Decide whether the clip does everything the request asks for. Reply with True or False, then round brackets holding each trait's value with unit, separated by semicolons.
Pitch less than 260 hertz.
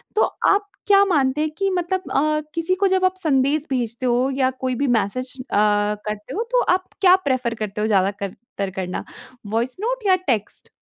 False (265 Hz)